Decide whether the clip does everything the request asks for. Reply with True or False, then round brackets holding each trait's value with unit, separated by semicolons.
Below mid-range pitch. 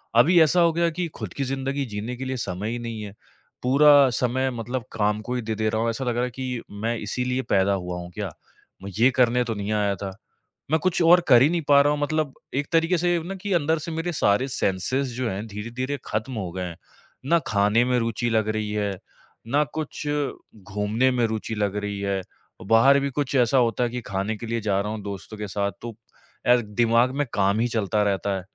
True (115 Hz)